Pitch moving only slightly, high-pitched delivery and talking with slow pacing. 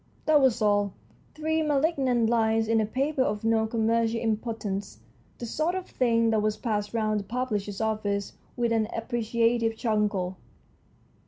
No: narrow, 2.2 semitones; high, 225 Hz; average, 150 wpm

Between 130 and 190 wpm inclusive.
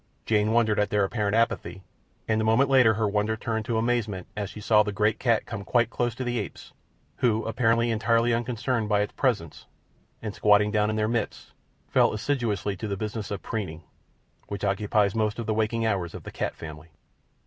No: average, 200 wpm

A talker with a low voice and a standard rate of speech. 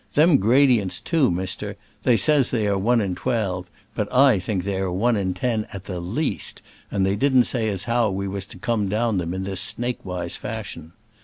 No: low, 105 Hz; fast, 210 wpm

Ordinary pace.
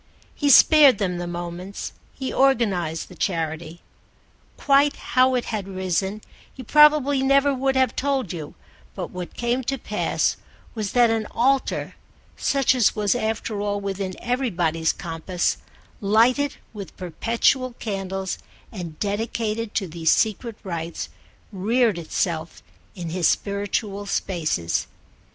No: slow, 130 wpm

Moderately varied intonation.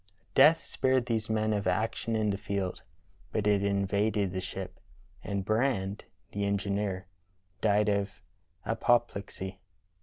No: narrow, 1.8 semitones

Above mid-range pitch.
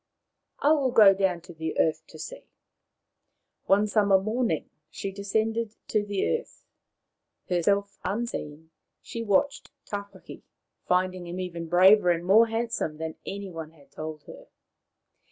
Yes: high, 195 Hz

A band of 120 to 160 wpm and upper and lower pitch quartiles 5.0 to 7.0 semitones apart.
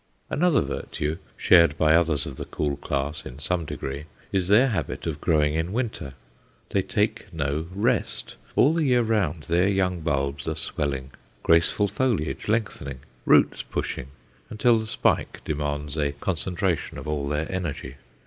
Yes: average, 155 wpm; wide, 5.6 semitones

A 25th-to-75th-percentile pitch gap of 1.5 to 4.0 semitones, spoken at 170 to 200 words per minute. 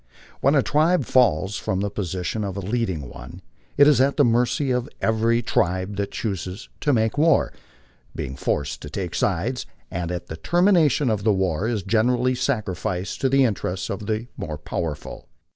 No: wide, 5.6 semitones; average, 175 wpm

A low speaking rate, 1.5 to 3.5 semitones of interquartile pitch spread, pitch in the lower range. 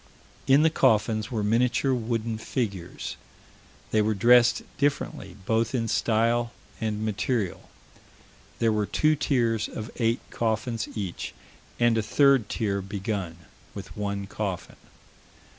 Yes: slow, 125 wpm; narrow, 2.4 semitones; low, 110 Hz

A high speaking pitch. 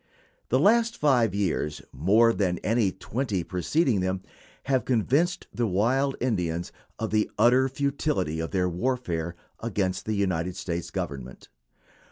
No: low, 105 Hz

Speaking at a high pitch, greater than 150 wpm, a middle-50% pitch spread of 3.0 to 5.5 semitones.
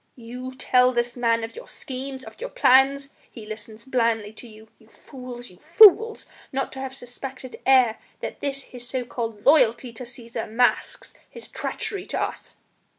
No: very high, 250 Hz; average, 170 wpm; narrow, 2.6 semitones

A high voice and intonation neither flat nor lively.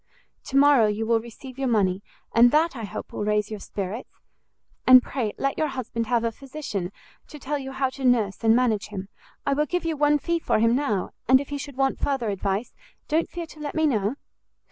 Yes: very high, 255 Hz; average, 4.8 semitones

